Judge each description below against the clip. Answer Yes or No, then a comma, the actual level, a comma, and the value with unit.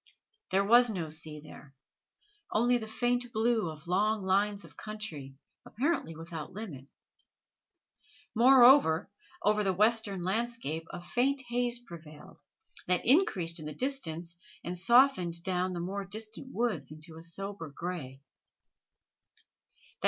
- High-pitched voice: Yes, high, 195 Hz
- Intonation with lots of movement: Yes, wide, 6.1 semitones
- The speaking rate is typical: No, slow, 125 wpm